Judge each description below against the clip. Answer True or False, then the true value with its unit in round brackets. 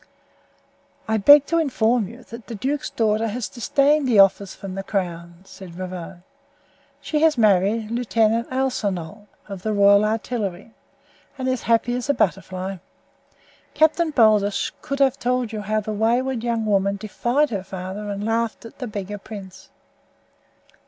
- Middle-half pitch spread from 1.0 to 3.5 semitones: False (3.9 semitones)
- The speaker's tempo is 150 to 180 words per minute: True (155 wpm)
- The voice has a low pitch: False (220 Hz)